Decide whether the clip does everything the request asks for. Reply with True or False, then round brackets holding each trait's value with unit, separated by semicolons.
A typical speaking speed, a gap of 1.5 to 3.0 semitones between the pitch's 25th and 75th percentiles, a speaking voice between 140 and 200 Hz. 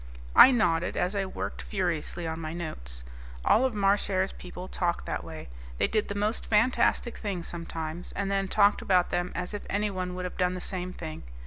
True (195 wpm; 2.7 semitones; 185 Hz)